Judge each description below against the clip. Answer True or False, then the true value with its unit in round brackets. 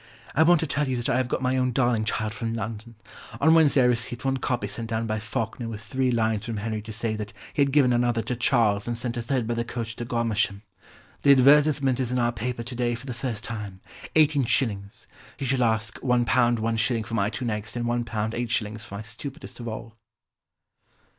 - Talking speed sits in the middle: False (220 wpm)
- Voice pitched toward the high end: False (120 Hz)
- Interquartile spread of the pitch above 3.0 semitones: False (2.4 semitones)